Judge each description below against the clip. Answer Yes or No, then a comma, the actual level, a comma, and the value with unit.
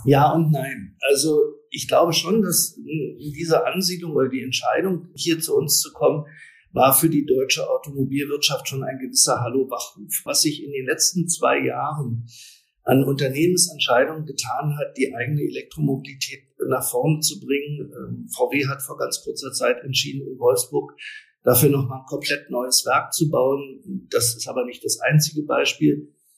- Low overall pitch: No, medium, 145 Hz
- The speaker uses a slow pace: No, average, 160 wpm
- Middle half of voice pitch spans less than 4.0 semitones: No, average, 4.4 semitones